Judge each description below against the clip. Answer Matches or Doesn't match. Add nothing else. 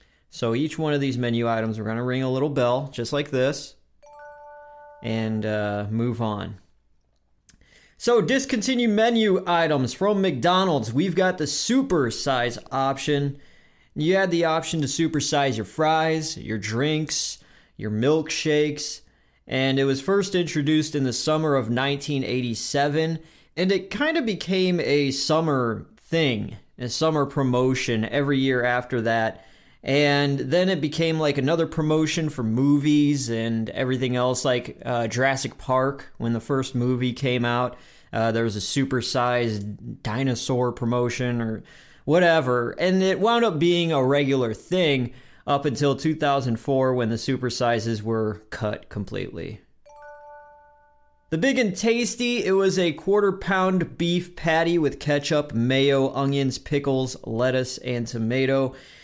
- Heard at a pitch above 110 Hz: Matches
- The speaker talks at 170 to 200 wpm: Doesn't match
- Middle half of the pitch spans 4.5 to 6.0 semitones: Matches